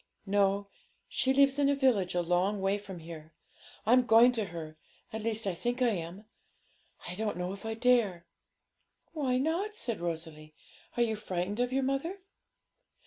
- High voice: Yes, high, 210 Hz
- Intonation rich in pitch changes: Yes, wide, 5.8 semitones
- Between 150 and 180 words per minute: Yes, average, 170 wpm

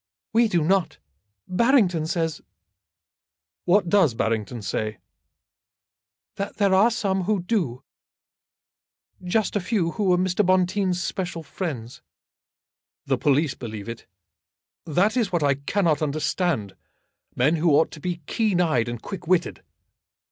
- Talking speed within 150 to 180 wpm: No, slow, 135 wpm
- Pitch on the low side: No, medium, 175 Hz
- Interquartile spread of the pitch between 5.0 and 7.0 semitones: Yes, average, 5.3 semitones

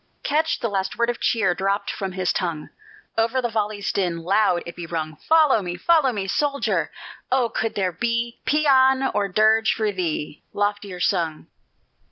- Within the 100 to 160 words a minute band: No, average, 170 wpm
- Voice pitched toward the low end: No, high, 205 Hz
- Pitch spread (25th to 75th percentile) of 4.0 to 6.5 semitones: Yes, average, 4.6 semitones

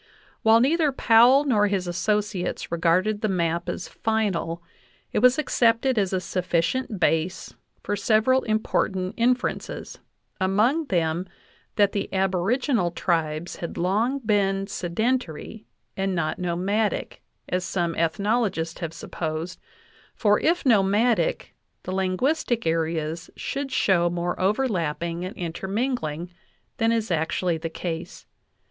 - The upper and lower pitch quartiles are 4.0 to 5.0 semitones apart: Yes, average, 4.7 semitones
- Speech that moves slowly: Yes, slow, 125 wpm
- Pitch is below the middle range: No, high, 190 Hz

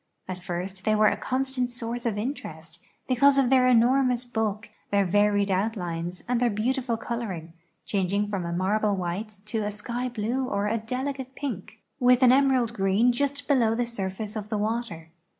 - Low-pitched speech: No, high, 220 Hz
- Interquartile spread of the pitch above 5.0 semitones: No, average, 3.8 semitones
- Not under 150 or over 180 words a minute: Yes, average, 175 wpm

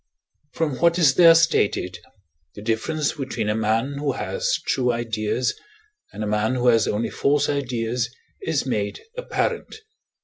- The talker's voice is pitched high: No, low, 125 Hz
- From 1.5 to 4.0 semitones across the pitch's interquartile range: No, average, 5.1 semitones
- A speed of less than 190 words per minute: Yes, average, 145 wpm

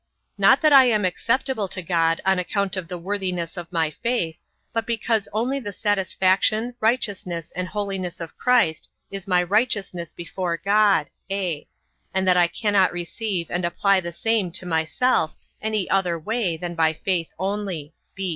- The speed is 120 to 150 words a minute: No, average, 160 wpm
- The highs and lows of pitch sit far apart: No, average, 3.7 semitones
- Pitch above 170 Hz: Yes, high, 190 Hz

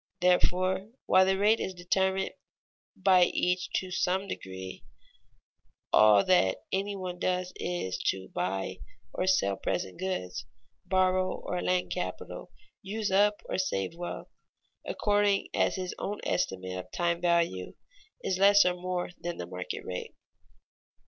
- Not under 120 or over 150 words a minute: Yes, slow, 135 wpm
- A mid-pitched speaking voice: Yes, medium, 180 Hz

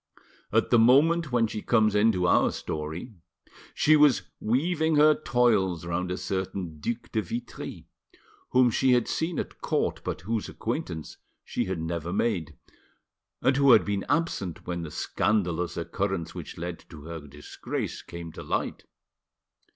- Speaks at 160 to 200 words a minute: No, average, 150 wpm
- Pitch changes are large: Yes, wide, 6.3 semitones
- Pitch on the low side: Yes, low, 100 Hz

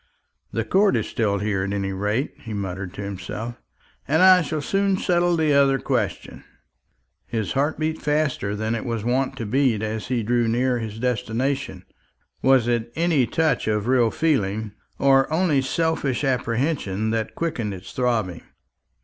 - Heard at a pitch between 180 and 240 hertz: No, low, 120 Hz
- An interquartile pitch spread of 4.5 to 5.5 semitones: Yes, average, 5.2 semitones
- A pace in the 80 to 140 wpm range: No, average, 160 wpm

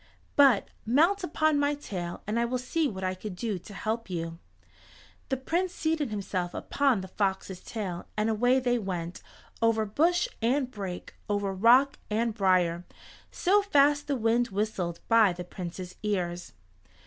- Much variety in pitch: Yes, wide, 6.4 semitones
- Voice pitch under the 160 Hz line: No, high, 220 Hz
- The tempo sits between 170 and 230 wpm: No, average, 160 wpm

